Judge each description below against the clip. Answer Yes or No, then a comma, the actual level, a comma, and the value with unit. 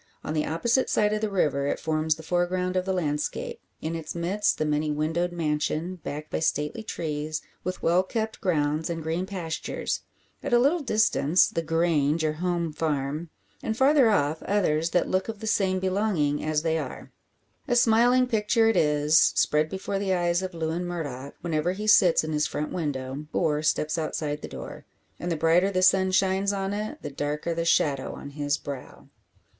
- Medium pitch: Yes, medium, 170 Hz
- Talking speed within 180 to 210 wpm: Yes, average, 190 wpm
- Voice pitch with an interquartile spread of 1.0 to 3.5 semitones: No, average, 4.1 semitones